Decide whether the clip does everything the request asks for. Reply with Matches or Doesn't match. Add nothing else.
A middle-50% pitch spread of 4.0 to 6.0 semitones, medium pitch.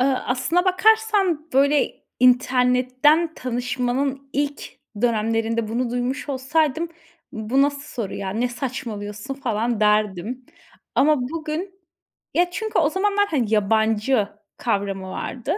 Doesn't match